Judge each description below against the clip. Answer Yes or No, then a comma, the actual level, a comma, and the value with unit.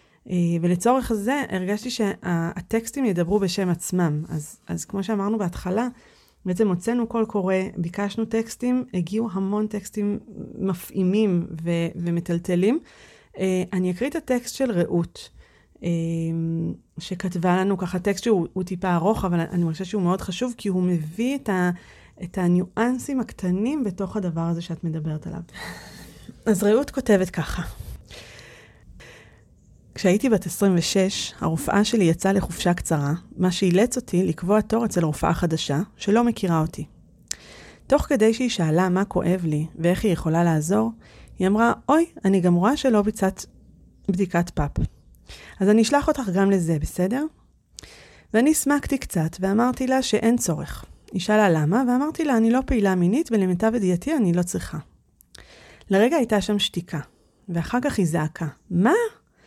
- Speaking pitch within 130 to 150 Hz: No, high, 190 Hz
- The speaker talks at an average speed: Yes, average, 140 wpm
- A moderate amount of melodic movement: Yes, average, 4.5 semitones